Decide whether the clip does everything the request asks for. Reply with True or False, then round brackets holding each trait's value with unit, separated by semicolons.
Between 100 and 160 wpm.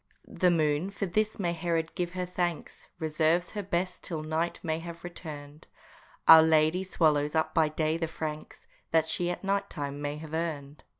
False (180 wpm)